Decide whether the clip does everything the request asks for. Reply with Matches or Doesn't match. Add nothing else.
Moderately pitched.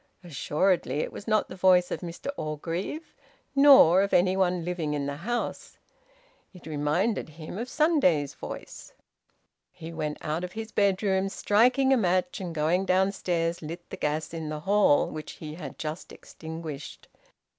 Matches